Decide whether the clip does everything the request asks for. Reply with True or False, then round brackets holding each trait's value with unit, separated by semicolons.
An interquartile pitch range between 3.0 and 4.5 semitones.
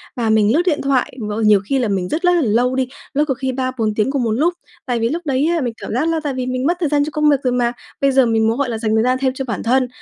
True (3.7 semitones)